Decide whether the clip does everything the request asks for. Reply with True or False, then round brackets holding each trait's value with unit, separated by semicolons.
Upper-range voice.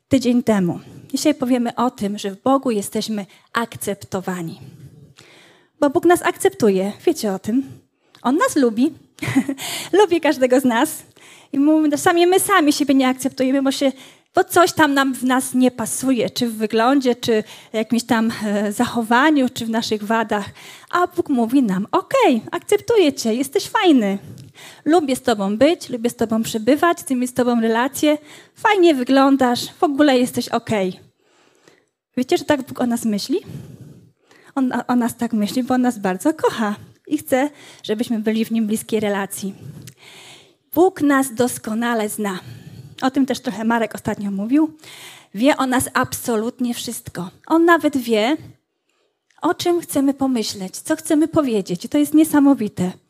True (250 Hz)